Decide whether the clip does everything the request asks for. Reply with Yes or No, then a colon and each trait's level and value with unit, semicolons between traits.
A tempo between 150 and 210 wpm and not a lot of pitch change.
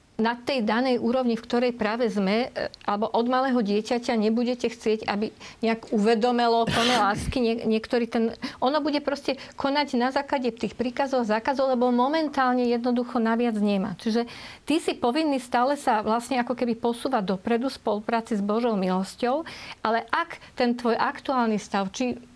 Yes: average, 160 wpm; narrow, 2.3 semitones